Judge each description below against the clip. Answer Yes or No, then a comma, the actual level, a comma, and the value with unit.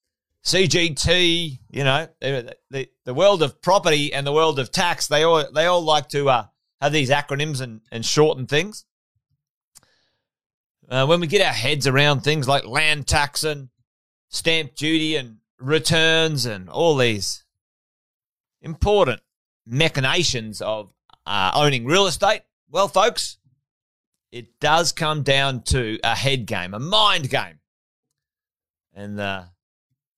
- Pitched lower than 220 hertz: Yes, medium, 140 Hz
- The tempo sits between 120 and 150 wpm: Yes, slow, 135 wpm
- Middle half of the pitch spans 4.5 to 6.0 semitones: Yes, average, 5.3 semitones